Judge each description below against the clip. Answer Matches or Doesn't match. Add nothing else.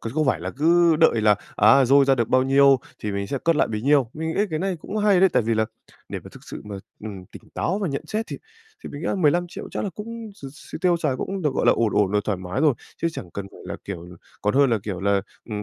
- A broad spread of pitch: Matches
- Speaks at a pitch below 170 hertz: Matches